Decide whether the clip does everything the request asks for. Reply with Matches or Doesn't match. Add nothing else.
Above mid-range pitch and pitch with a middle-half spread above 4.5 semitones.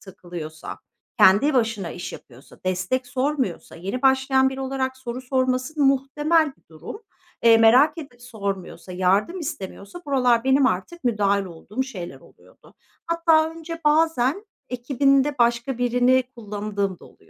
Matches